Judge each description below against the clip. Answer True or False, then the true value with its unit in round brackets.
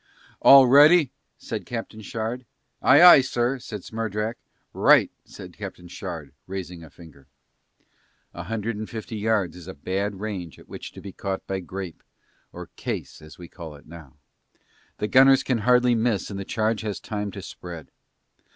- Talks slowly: False (170 wpm)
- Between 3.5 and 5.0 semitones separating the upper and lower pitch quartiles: True (4.6 semitones)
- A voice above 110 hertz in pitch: False (105 Hz)